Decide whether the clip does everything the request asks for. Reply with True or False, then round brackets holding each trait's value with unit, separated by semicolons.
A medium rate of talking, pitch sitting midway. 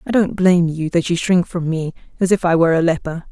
False (270 wpm; 170 Hz)